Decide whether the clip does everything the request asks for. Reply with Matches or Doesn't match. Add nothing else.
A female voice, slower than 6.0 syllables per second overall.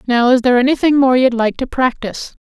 Doesn't match